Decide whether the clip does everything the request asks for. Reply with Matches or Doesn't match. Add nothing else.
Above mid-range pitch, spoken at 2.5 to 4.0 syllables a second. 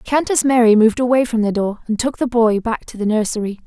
Doesn't match